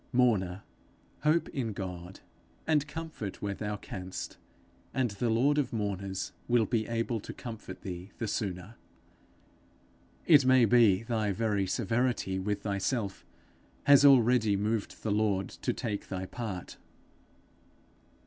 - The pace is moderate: No, slow, 130 wpm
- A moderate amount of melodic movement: Yes, average, 3.8 semitones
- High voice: No, low, 110 Hz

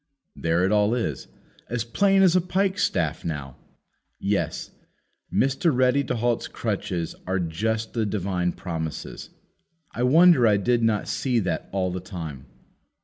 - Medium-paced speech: Yes, average, 145 wpm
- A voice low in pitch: Yes, low, 105 Hz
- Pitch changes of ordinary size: No, wide, 6.0 semitones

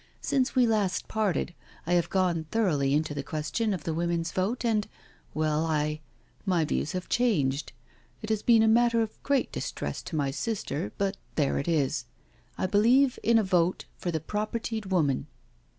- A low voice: No, medium, 185 Hz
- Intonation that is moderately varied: No, wide, 6.1 semitones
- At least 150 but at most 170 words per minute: No, average, 180 wpm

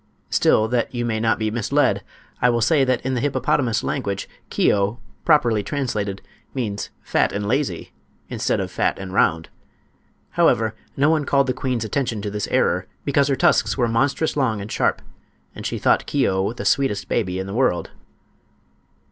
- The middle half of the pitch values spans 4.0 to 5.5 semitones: Yes, average, 4.4 semitones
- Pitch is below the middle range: Yes, low, 115 Hz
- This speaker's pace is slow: No, average, 175 wpm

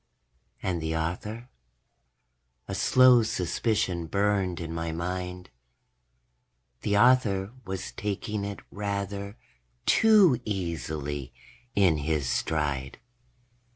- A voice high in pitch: No, very low, 95 Hz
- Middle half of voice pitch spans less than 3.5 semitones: No, average, 4.2 semitones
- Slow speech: Yes, slow, 90 wpm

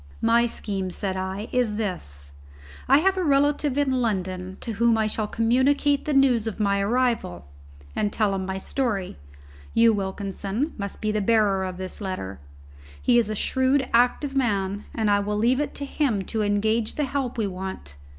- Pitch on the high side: Yes, high, 215 Hz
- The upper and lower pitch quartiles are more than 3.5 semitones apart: Yes, average, 4.5 semitones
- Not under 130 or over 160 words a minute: No, average, 180 wpm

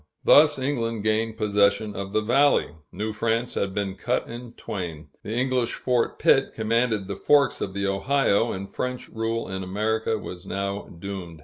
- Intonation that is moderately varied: Yes, average, 3.3 semitones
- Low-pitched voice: Yes, low, 110 Hz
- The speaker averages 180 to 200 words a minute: No, average, 170 wpm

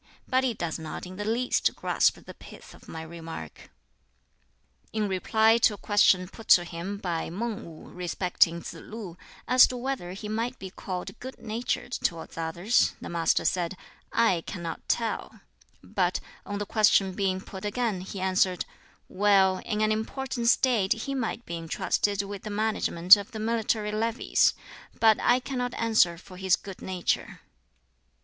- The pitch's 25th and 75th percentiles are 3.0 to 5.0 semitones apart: Yes, average, 3.9 semitones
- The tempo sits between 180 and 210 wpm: No, average, 165 wpm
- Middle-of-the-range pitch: No, high, 205 Hz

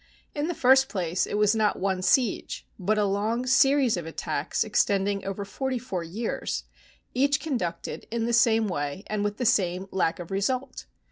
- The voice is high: Yes, high, 210 Hz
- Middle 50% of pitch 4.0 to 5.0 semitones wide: Yes, average, 4.7 semitones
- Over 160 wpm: Yes, average, 180 wpm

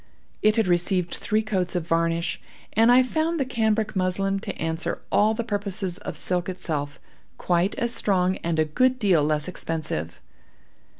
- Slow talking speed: No, average, 165 wpm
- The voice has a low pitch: No, medium, 185 Hz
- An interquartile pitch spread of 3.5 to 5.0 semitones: Yes, average, 4.6 semitones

